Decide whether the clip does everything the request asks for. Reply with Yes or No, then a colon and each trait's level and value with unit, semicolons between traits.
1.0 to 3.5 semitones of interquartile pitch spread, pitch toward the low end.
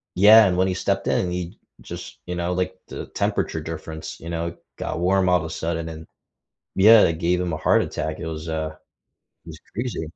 Yes: narrow, 2.5 semitones; very low, 85 Hz